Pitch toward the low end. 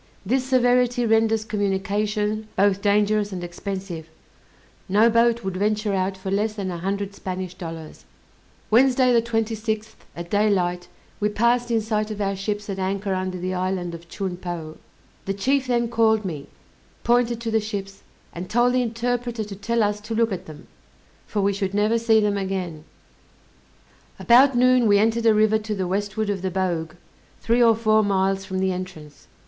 No: high, 205 Hz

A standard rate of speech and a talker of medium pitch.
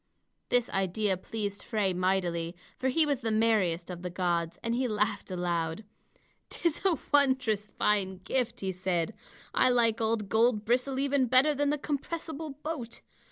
No: average, 155 wpm; high, 220 Hz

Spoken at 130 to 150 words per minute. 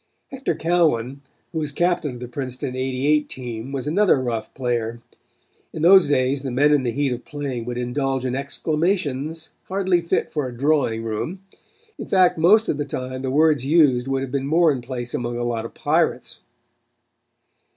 No: average, 180 wpm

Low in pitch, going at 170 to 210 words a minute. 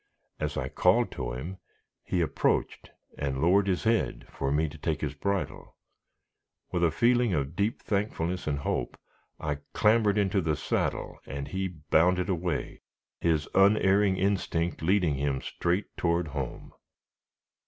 No: very low, 85 Hz; average, 145 wpm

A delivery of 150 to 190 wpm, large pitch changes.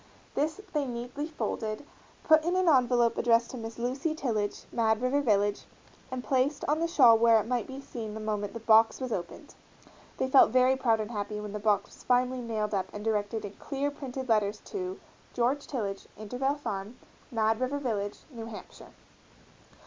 No: average, 185 wpm; average, 3.8 semitones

